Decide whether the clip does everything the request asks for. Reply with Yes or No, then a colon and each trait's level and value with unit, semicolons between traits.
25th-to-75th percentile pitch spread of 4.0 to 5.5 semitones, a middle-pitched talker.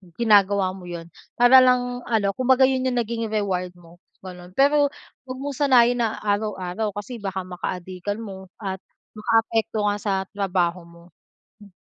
No: average, 4.4 semitones; high, 205 Hz